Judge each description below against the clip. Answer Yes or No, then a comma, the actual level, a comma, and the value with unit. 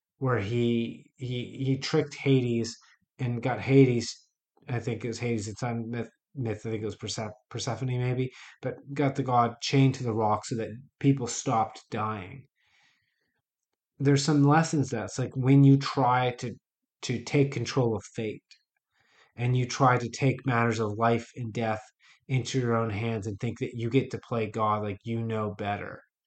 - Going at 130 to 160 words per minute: No, average, 180 wpm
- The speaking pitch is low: Yes, low, 120 Hz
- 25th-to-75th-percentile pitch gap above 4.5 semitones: No, narrow, 2.6 semitones